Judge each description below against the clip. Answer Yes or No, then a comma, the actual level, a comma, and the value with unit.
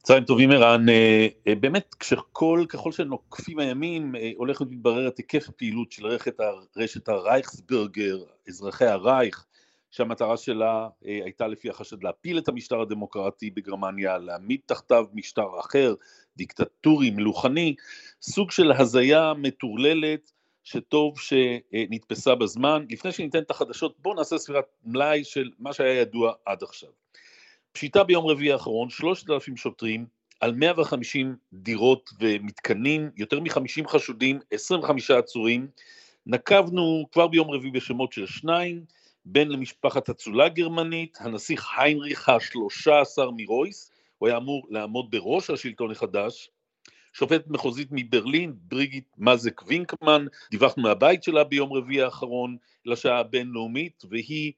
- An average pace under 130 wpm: Yes, average, 120 wpm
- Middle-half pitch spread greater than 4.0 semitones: Yes, average, 5.0 semitones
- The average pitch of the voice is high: No, low, 135 Hz